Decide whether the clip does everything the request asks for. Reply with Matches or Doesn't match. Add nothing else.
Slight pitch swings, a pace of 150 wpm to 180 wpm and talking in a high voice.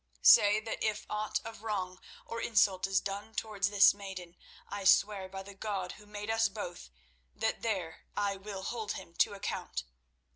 Matches